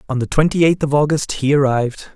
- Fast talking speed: Yes, fast, 225 wpm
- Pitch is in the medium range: Yes, medium, 145 Hz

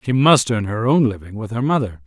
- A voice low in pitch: Yes, low, 120 Hz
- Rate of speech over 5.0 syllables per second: Yes, 5.7 syllables/s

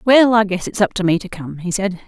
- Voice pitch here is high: Yes, high, 195 Hz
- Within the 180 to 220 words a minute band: No, fast, 320 wpm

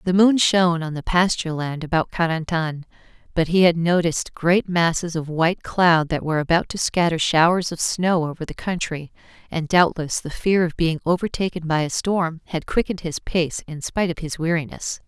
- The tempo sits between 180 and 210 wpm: Yes, average, 190 wpm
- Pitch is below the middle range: No, medium, 170 Hz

